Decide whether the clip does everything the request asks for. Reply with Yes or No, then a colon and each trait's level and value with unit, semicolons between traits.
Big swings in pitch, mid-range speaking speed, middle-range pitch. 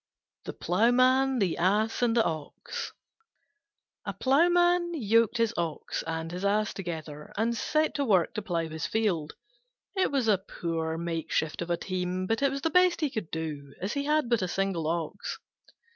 No: wide, 7.3 semitones; average, 175 wpm; high, 200 Hz